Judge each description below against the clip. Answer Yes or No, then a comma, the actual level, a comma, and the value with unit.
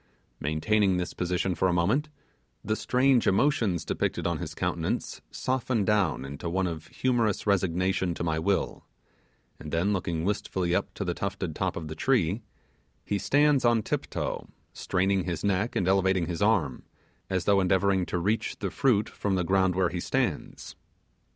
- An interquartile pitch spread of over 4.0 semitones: No, average, 3.1 semitones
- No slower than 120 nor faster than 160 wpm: No, average, 170 wpm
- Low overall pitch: Yes, very low, 95 Hz